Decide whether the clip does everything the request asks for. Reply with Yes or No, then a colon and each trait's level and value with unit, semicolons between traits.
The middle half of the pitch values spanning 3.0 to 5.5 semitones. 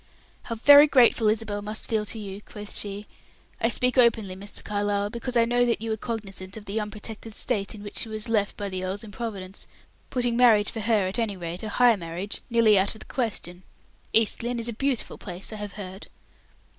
No: narrow, 2.5 semitones